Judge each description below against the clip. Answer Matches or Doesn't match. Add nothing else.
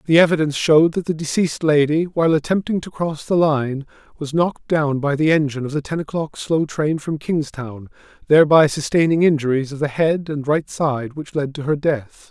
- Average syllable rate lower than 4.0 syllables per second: Doesn't match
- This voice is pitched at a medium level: Matches